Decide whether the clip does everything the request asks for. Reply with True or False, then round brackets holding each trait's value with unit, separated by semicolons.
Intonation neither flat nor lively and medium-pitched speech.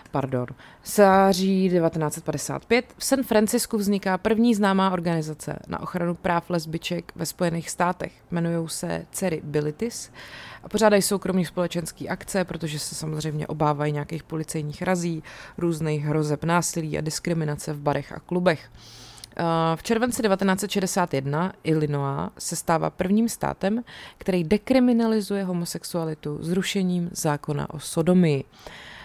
True (3.9 semitones; 170 Hz)